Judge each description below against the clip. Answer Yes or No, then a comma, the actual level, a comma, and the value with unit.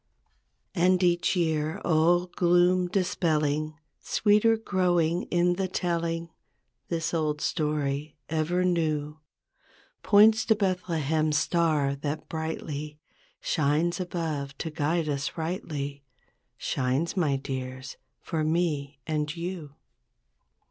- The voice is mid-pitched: Yes, medium, 160 Hz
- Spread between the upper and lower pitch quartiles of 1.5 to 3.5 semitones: Yes, average, 2.9 semitones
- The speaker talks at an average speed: No, slow, 100 wpm